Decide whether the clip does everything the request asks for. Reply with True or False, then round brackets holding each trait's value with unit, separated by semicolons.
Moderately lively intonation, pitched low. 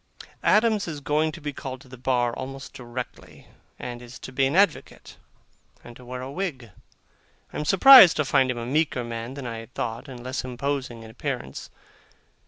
True (3.4 semitones; 130 Hz)